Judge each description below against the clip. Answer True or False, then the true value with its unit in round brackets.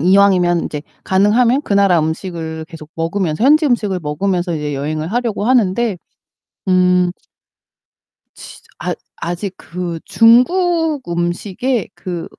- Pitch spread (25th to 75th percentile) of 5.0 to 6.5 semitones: True (5.4 semitones)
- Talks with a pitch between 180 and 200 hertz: True (185 Hz)